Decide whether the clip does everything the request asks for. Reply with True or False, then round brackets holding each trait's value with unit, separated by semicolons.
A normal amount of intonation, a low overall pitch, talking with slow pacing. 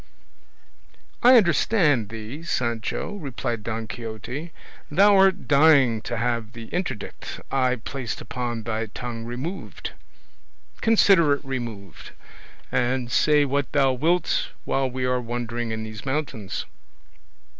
True (4.5 semitones; 125 Hz; 120 wpm)